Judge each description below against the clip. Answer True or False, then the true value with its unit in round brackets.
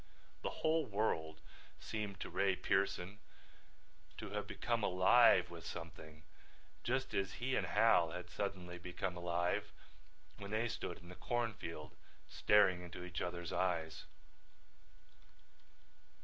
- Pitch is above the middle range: False (90 Hz)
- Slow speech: True (125 wpm)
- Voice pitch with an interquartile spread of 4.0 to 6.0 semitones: False (3.5 semitones)